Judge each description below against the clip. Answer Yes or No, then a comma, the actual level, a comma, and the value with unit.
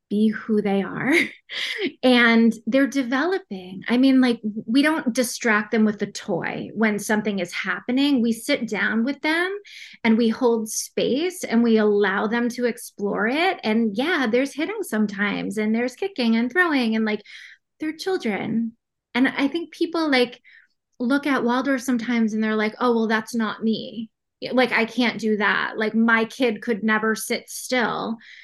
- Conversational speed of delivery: Yes, average, 170 wpm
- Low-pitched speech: No, high, 235 Hz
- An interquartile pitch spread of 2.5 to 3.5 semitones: Yes, average, 3.1 semitones